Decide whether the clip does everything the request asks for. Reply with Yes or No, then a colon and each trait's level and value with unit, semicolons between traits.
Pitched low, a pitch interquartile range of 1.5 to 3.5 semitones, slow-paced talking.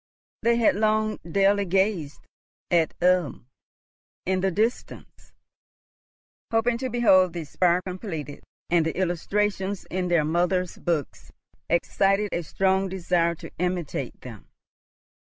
No: medium, 185 Hz; average, 2.8 semitones; slow, 120 wpm